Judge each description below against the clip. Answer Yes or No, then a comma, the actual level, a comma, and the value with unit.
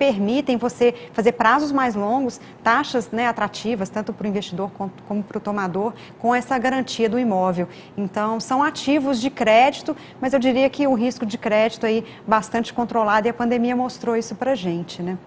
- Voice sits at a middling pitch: No, high, 230 Hz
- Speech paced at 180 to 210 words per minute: Yes, fast, 185 wpm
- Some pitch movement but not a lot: Yes, average, 3.3 semitones